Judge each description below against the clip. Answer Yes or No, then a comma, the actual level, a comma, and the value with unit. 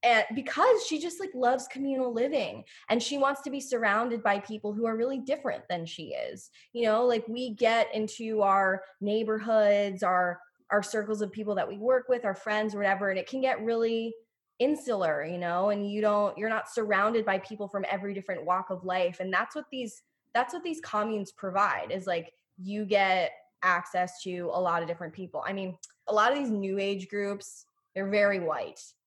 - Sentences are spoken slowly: No, average, 200 wpm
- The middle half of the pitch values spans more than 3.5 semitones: Yes, average, 4.0 semitones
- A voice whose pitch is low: No, high, 210 Hz